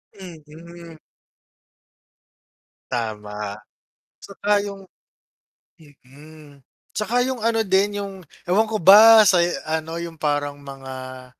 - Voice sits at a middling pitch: Yes, medium, 165 Hz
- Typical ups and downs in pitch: No, wide, 5.9 semitones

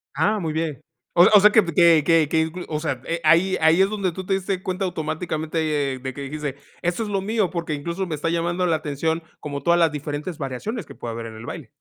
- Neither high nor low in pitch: Yes, medium, 165 Hz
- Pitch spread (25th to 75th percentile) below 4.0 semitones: Yes, average, 3.3 semitones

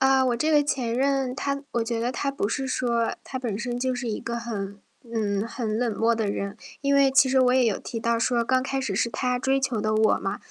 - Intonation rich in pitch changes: No, average, 2.8 semitones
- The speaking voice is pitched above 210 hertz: Yes, high, 240 Hz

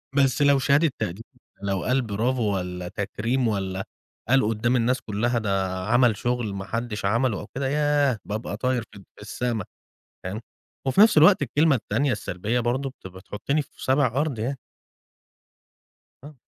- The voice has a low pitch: Yes, low, 120 Hz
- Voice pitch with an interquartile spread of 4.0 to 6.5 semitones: Yes, average, 4.5 semitones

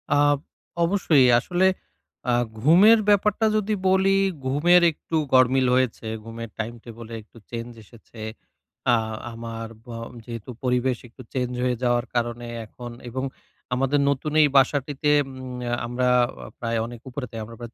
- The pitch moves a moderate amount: Yes, average, 3.7 semitones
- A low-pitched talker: Yes, low, 125 Hz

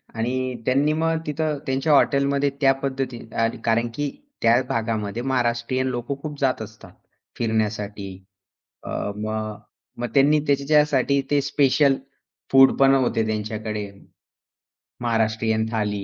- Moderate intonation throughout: Yes, average, 4.0 semitones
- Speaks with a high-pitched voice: No, low, 125 Hz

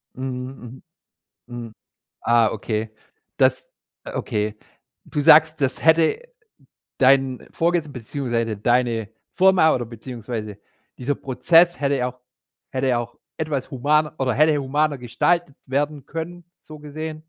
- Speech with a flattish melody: No, average, 4.2 semitones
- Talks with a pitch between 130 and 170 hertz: Yes, low, 135 Hz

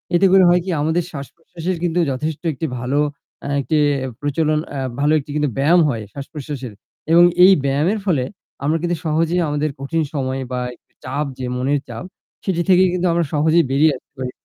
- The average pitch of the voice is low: No, medium, 155 Hz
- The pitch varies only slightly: No, average, 3.7 semitones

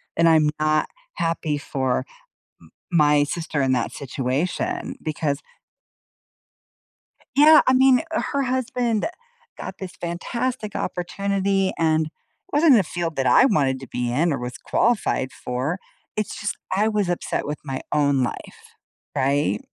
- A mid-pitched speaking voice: Yes, medium, 165 Hz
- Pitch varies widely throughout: Yes, wide, 6.8 semitones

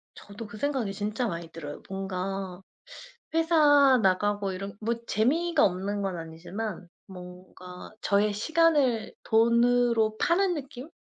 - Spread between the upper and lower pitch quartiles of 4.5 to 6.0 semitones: Yes, average, 5.1 semitones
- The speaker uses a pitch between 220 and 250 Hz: No, high, 210 Hz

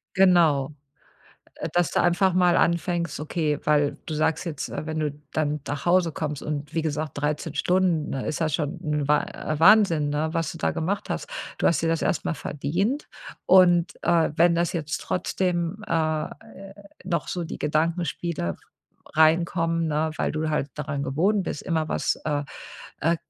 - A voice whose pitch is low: No, medium, 160 Hz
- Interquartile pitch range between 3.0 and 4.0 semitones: No, narrow, 2.4 semitones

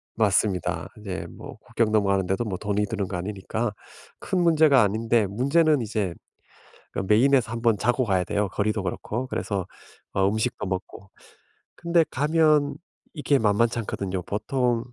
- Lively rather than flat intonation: No, average, 4.6 semitones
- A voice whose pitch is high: No, low, 110 Hz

